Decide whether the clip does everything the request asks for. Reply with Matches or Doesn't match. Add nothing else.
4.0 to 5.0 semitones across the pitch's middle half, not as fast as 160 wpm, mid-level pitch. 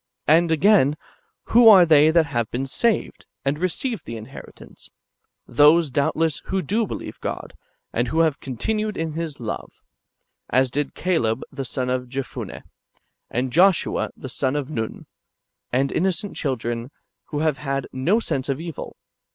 Matches